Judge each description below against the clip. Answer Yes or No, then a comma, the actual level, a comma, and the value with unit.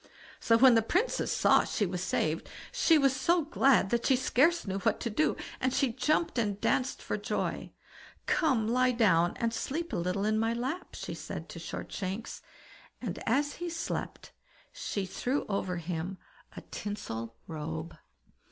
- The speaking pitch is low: No, high, 230 Hz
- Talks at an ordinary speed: Yes, average, 165 wpm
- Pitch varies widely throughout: Yes, wide, 6.3 semitones